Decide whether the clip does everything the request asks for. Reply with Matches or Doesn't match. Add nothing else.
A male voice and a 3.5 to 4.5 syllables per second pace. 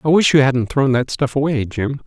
Doesn't match